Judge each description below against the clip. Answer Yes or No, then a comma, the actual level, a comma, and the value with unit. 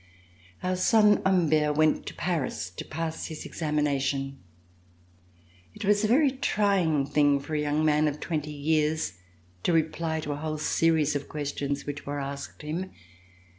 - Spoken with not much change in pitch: Yes, narrow, 2.3 semitones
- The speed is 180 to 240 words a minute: No, average, 160 wpm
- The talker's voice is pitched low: No, medium, 155 Hz